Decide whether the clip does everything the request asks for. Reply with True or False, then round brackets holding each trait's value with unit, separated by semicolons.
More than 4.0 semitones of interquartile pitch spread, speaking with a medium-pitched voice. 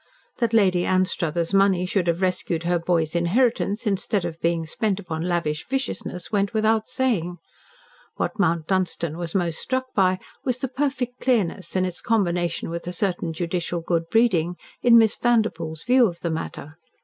True (4.6 semitones; 180 Hz)